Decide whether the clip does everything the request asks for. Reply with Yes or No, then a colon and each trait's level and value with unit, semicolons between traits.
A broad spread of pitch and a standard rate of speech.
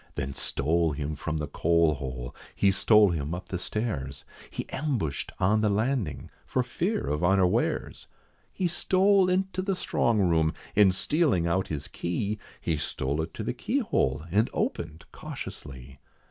Yes: wide, 6.3 semitones; average, 155 wpm